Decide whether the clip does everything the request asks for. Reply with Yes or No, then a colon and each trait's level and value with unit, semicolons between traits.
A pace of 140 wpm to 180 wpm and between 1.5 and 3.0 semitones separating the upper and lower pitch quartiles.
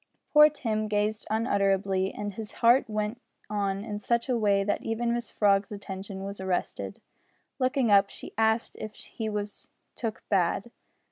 Yes: average, 155 wpm; narrow, 2.5 semitones